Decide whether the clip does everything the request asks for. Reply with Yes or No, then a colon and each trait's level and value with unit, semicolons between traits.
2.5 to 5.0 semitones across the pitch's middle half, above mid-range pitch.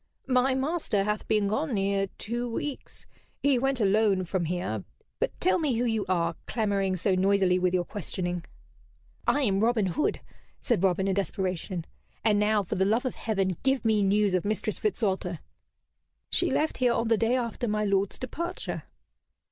Yes: average, 4.0 semitones; high, 210 Hz